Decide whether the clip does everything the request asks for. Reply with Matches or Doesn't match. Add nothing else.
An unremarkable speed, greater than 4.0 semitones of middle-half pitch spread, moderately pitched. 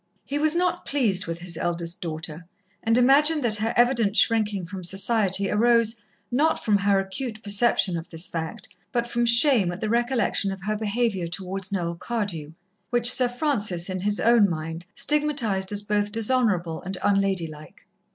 Doesn't match